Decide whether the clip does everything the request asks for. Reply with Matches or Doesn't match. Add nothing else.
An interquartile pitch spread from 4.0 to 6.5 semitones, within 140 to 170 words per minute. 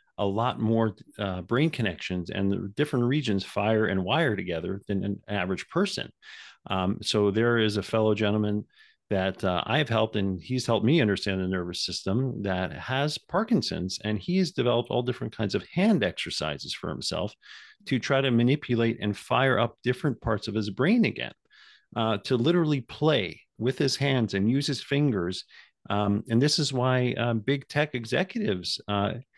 Doesn't match